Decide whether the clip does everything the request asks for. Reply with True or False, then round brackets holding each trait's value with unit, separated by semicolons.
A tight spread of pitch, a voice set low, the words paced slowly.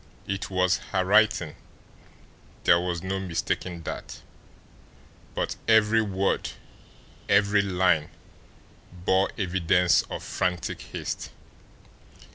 True (2.0 semitones; 95 Hz; 90 wpm)